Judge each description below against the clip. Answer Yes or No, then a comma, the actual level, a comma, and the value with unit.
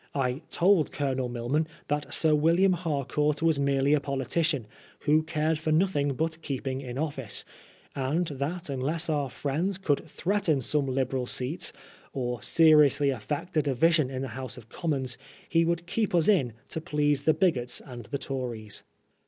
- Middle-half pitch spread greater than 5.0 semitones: No, average, 3.5 semitones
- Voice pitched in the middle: Yes, medium, 145 Hz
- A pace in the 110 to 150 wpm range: No, average, 165 wpm